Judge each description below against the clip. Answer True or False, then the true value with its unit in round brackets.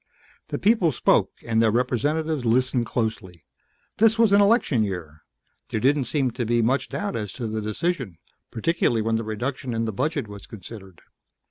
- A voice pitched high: False (120 Hz)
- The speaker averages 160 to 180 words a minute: True (170 wpm)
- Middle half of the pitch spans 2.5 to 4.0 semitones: False (5.3 semitones)